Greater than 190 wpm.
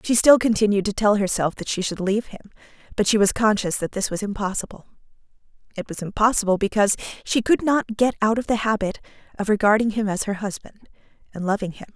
Yes: average, 200 wpm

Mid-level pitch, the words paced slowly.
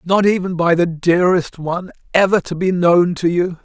No: medium, 175 Hz; average, 200 wpm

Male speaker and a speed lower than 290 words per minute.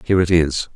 Yes: male; fast, 240 wpm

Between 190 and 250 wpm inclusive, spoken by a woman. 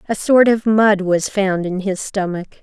Yes: fast, 205 wpm; female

